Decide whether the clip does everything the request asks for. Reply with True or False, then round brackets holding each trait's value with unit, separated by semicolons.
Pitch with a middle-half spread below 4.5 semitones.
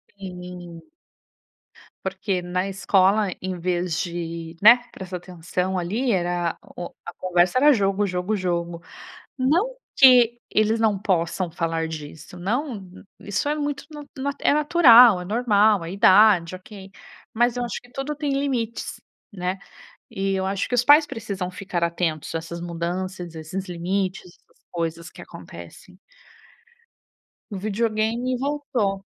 False (4.8 semitones)